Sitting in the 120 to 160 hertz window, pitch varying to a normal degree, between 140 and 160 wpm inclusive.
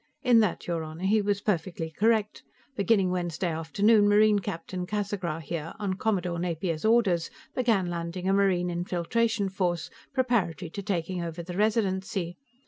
No: medium, 185 Hz; average, 3.5 semitones; average, 145 wpm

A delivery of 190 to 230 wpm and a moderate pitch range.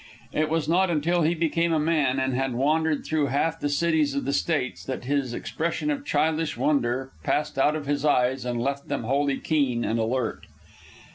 Yes: average, 195 wpm; average, 3.2 semitones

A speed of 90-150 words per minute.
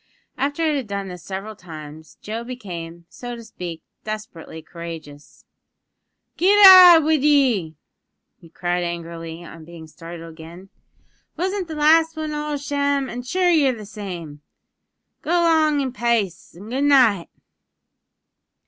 Yes: average, 140 wpm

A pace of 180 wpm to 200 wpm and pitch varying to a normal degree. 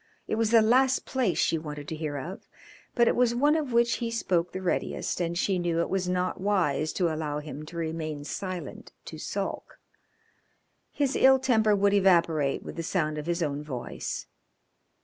No: average, 190 wpm; wide, 6.3 semitones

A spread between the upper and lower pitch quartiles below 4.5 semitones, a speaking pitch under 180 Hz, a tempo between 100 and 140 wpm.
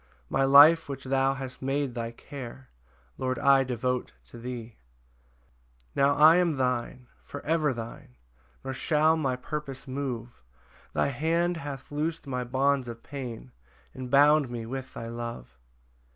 No: narrow, 2.6 semitones; low, 135 Hz; average, 150 wpm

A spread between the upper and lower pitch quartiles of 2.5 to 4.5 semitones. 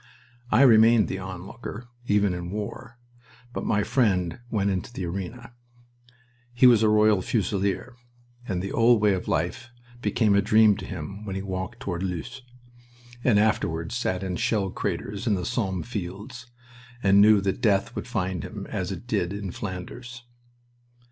Yes: average, 3.5 semitones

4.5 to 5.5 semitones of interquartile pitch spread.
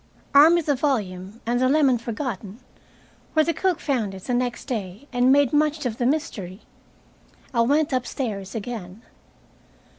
Yes: average, 5.1 semitones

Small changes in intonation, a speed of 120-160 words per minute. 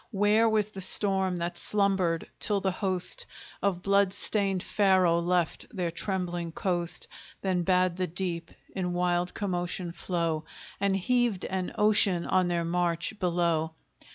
Yes: narrow, 2.1 semitones; average, 140 wpm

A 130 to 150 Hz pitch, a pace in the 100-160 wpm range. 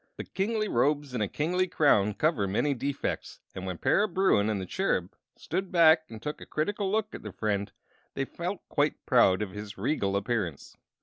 No: medium, 140 Hz; average, 190 wpm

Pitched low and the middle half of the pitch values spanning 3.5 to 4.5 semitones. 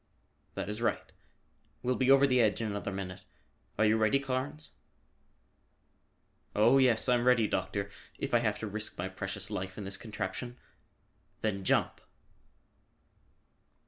Yes: low, 110 Hz; average, 4.0 semitones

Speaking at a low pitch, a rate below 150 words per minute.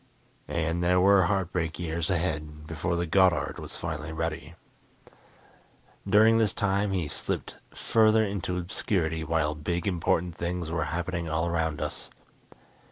Yes: very low, 85 Hz; slow, 135 wpm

